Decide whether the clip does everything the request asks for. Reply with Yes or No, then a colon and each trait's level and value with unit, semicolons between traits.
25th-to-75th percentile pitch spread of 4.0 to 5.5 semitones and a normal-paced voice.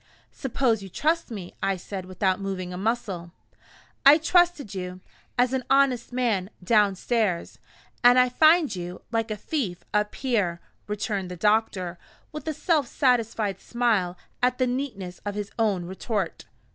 Yes: average, 5.1 semitones; average, 150 wpm